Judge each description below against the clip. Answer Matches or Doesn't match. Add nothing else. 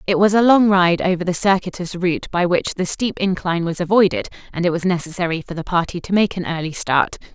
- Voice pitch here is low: Doesn't match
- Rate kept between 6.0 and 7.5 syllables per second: Matches